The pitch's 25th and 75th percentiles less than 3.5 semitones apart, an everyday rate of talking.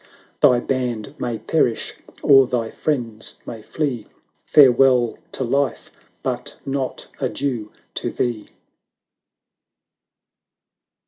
No: average, 2.9 semitones; slow, 105 wpm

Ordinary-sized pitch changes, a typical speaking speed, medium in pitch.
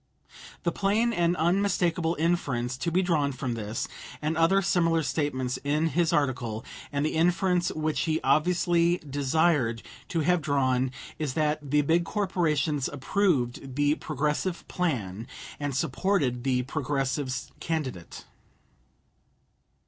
No: average, 4.6 semitones; slow, 125 wpm; medium, 150 Hz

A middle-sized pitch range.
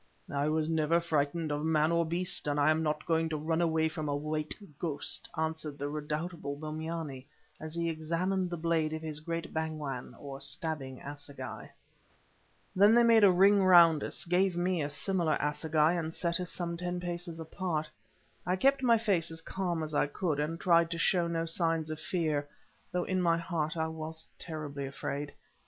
No: narrow, 2.1 semitones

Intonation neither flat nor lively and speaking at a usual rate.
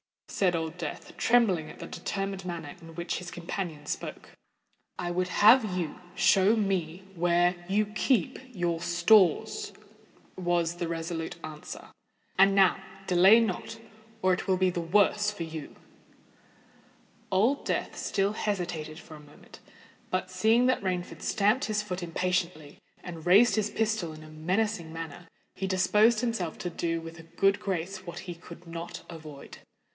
Yes: average, 3.3 semitones; average, 150 wpm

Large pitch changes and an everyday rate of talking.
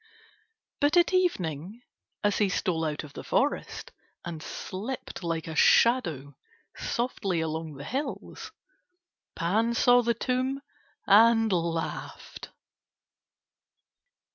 No: wide, 7.0 semitones; slow, 105 wpm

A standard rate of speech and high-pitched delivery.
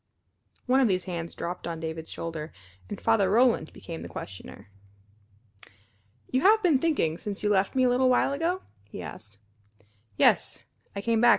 Yes: average, 170 wpm; high, 200 Hz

